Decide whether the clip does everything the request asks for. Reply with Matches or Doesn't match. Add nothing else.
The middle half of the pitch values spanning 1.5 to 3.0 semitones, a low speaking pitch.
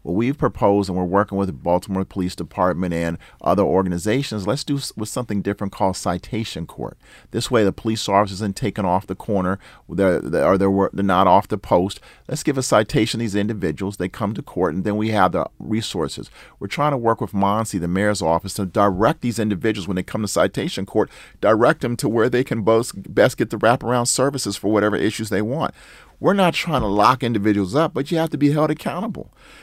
Doesn't match